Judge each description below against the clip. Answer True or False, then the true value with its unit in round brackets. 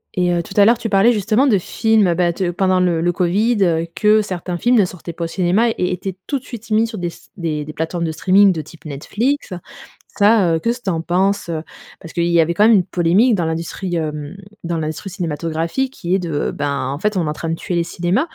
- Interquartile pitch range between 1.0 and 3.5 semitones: False (3.9 semitones)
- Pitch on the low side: False (180 Hz)